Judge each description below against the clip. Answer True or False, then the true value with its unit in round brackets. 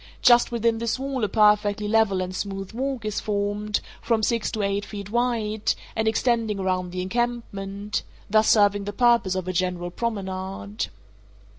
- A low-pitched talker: False (210 Hz)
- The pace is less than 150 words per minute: False (155 wpm)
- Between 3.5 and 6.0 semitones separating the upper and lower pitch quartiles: False (2.8 semitones)